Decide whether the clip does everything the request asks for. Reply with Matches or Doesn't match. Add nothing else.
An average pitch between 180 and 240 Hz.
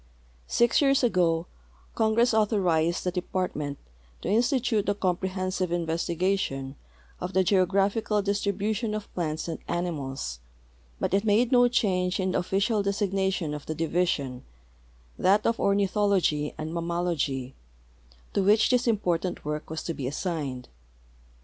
Matches